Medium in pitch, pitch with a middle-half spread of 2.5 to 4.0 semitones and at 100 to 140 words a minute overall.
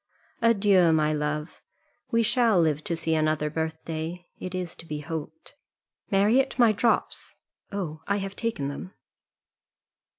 No: medium, 170 Hz; average, 4.5 semitones; slow, 135 wpm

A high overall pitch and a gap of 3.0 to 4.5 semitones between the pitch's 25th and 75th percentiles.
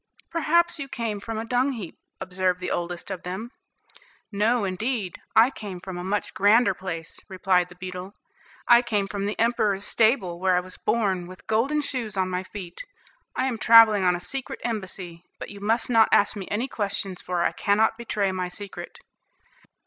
Yes: high, 205 Hz; average, 3.8 semitones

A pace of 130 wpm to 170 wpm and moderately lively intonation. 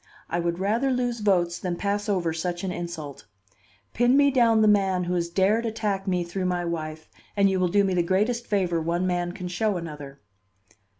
No: average, 200 wpm; average, 3.3 semitones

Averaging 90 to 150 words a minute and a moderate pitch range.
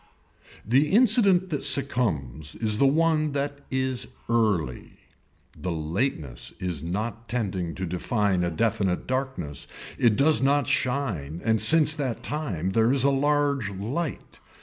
No: slow, 135 wpm; wide, 7.4 semitones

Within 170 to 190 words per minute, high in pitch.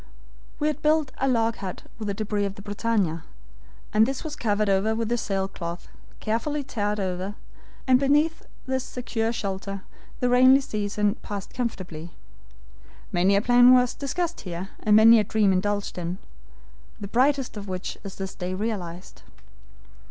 No: average, 160 wpm; high, 210 Hz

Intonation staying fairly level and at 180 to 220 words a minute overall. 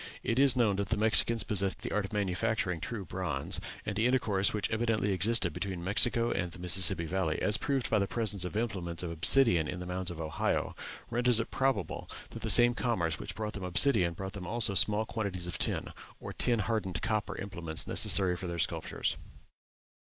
No: average, 4.1 semitones; average, 200 wpm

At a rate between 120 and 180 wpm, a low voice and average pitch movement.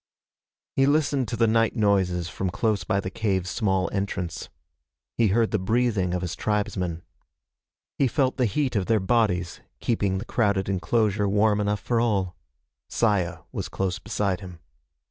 Yes: average, 160 wpm; low, 100 Hz; average, 3.4 semitones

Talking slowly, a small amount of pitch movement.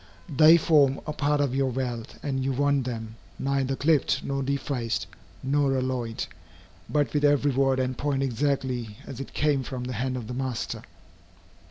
No: average, 170 wpm; narrow, 2.1 semitones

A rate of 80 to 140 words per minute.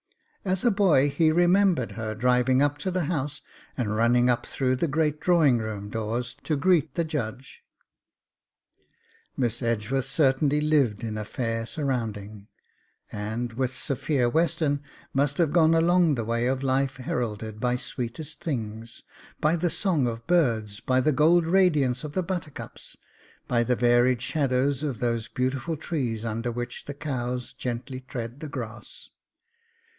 No: average, 150 wpm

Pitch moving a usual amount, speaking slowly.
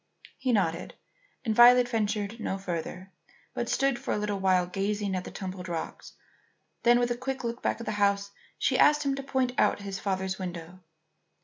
No: average, 4.2 semitones; average, 190 wpm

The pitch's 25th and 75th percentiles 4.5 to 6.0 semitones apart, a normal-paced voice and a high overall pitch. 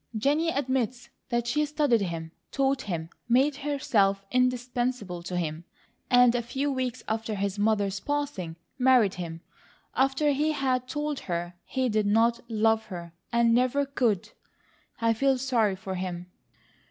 Yes: average, 5.1 semitones; average, 145 wpm; high, 235 Hz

